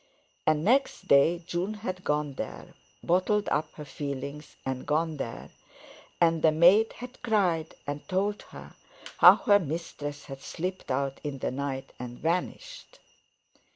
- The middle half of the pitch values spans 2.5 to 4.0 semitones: No, average, 4.9 semitones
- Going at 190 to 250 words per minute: No, average, 140 wpm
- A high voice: No, medium, 160 Hz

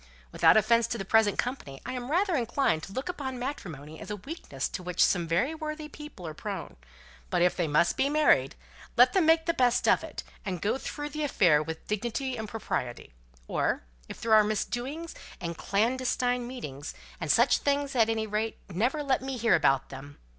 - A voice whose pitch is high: Yes, high, 230 Hz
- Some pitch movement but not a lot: No, wide, 7.3 semitones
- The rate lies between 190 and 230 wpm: Yes, average, 195 wpm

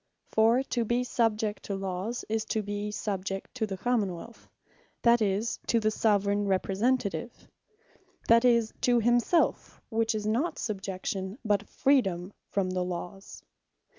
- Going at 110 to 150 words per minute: Yes, average, 140 wpm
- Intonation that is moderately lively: Yes, average, 3.1 semitones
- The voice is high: Yes, high, 215 Hz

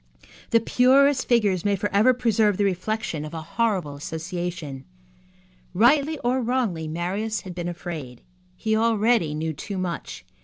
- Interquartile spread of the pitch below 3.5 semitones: No, wide, 5.4 semitones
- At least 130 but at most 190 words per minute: Yes, average, 140 wpm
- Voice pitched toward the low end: No, high, 200 Hz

